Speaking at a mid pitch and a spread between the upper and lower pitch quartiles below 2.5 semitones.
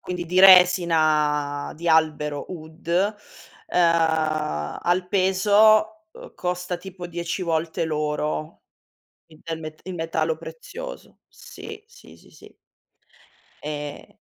No: medium, 165 Hz; average, 2.9 semitones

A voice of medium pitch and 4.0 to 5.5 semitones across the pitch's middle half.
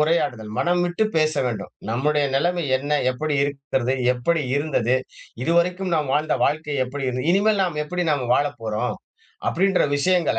Yes: medium, 150 Hz; average, 4.7 semitones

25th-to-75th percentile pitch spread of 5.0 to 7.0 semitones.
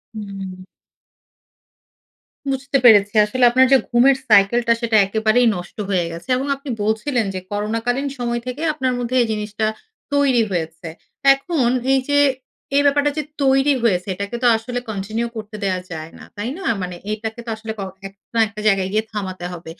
No: average, 4.3 semitones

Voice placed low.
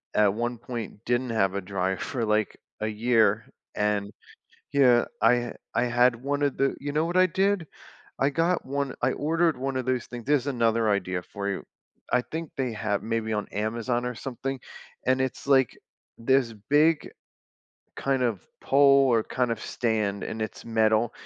Yes: low, 120 Hz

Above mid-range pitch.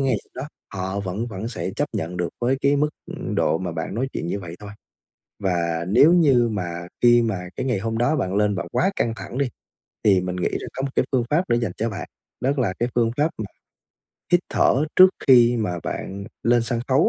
No: low, 115 Hz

